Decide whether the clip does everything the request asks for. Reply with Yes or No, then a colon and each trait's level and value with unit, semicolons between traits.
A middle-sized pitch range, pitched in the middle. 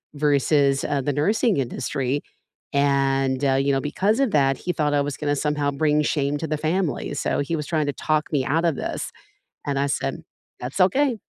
No: narrow, 2.1 semitones; medium, 145 Hz